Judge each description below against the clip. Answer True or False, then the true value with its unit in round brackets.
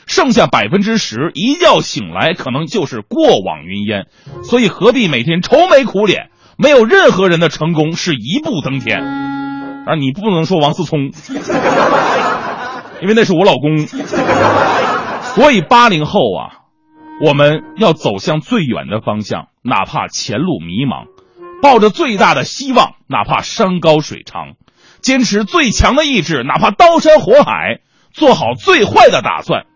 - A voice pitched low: False (205 Hz)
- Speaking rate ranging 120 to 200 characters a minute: False (225 characters per minute)